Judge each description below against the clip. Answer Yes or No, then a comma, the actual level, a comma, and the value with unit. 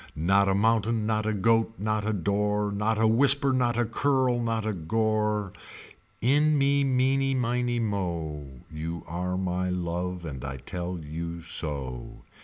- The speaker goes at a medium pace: Yes, average, 155 wpm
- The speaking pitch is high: No, low, 105 Hz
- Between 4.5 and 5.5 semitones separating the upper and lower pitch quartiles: Yes, average, 5.2 semitones